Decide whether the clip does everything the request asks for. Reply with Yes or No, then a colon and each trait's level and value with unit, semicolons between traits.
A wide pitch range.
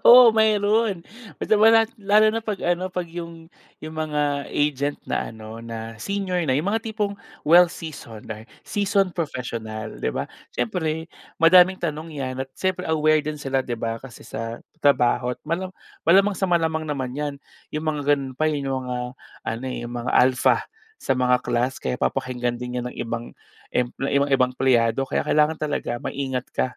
Yes: wide, 5.9 semitones